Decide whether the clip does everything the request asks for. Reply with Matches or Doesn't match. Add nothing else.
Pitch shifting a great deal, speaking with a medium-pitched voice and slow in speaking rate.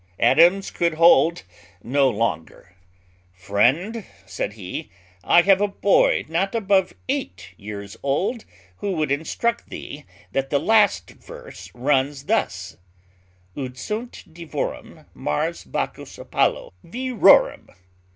Matches